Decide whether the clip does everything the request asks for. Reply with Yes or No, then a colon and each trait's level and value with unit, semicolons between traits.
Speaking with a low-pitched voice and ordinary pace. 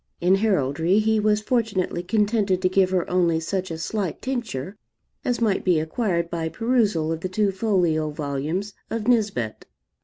No: medium, 185 Hz; average, 160 wpm